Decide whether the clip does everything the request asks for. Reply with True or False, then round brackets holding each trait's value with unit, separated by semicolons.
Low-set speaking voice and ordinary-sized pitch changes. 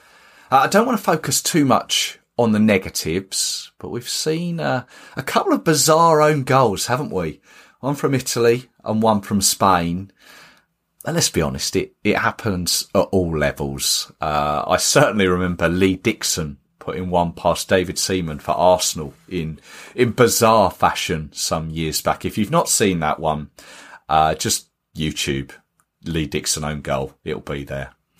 False (90 Hz; 6.4 semitones)